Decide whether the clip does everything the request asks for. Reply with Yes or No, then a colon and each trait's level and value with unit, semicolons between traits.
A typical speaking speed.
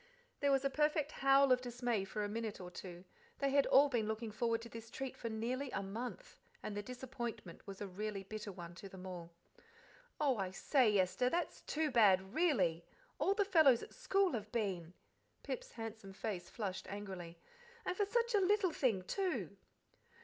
Yes: average, 185 wpm